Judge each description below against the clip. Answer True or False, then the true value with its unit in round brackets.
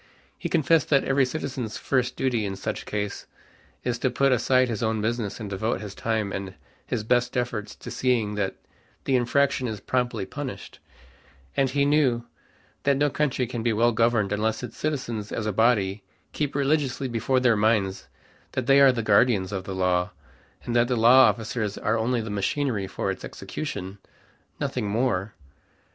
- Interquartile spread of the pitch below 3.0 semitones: False (3.7 semitones)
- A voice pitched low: True (120 Hz)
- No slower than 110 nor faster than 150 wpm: False (175 wpm)